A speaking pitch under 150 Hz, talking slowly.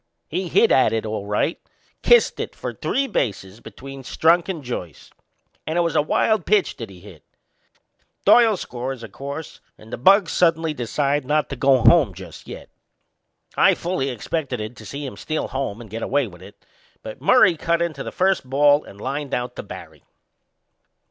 No: medium, 140 Hz; average, 180 wpm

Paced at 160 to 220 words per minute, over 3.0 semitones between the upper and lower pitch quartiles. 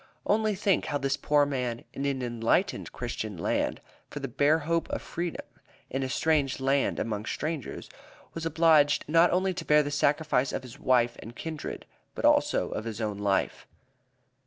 Yes: average, 175 wpm; average, 4.7 semitones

